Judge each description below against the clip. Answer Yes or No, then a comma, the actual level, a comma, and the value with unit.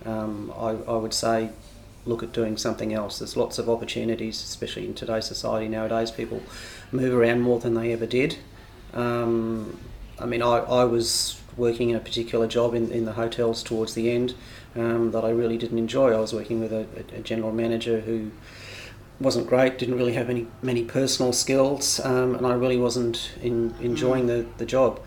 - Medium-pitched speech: No, low, 115 Hz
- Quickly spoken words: No, average, 190 wpm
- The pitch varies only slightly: Yes, narrow, 1.2 semitones